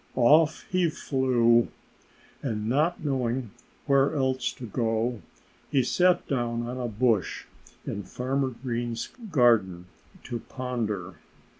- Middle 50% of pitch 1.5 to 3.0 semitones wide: Yes, average, 2.7 semitones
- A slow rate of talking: Yes, slow, 115 wpm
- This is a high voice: No, low, 125 Hz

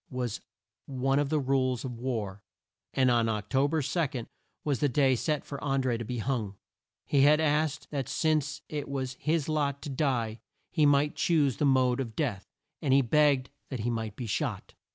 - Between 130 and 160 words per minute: No, average, 190 wpm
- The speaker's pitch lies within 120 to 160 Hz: Yes, low, 135 Hz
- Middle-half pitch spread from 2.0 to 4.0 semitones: Yes, average, 3.1 semitones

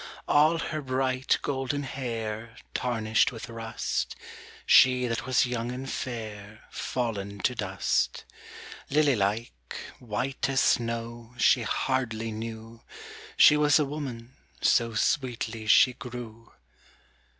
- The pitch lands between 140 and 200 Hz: No, low, 120 Hz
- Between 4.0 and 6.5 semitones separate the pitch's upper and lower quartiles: No, narrow, 2.6 semitones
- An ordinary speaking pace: No, slow, 115 wpm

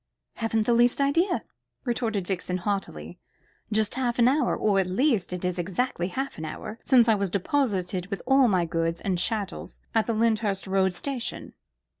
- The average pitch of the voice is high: Yes, high, 210 Hz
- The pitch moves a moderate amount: Yes, average, 4.7 semitones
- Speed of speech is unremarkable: Yes, average, 175 wpm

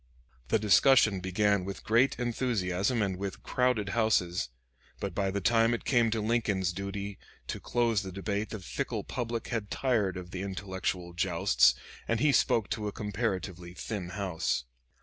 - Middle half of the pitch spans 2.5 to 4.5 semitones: Yes, average, 3.4 semitones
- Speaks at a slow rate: No, average, 160 wpm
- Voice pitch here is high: No, low, 100 Hz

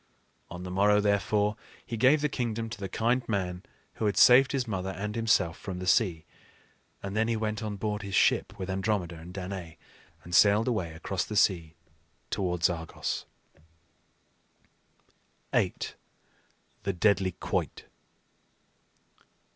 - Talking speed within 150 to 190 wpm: No, average, 140 wpm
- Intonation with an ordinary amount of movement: Yes, average, 3.2 semitones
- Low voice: Yes, low, 100 Hz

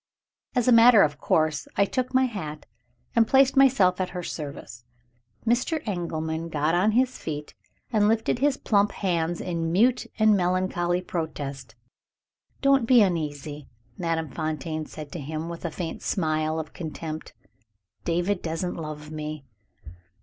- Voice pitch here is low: No, medium, 170 Hz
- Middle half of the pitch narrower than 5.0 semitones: No, average, 5.3 semitones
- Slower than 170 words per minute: Yes, average, 145 wpm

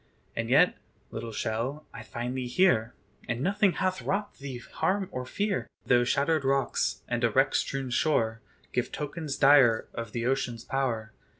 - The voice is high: No, low, 135 Hz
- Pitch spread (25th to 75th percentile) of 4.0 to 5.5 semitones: Yes, average, 4.8 semitones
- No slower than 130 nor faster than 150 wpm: No, average, 165 wpm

